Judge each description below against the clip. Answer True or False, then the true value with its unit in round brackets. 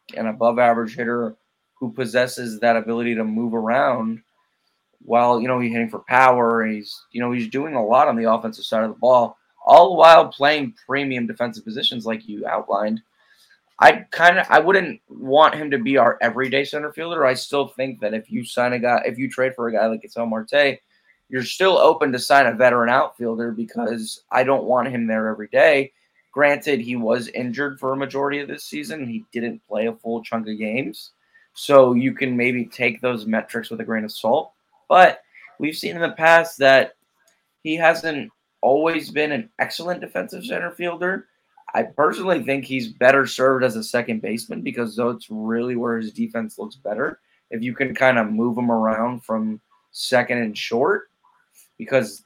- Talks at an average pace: True (190 wpm)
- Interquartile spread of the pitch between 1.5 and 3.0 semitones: False (3.4 semitones)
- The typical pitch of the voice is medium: False (120 Hz)